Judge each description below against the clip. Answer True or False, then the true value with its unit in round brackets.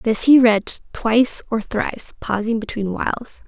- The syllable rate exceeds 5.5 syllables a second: False (4.6 syllables/s)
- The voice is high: True (225 Hz)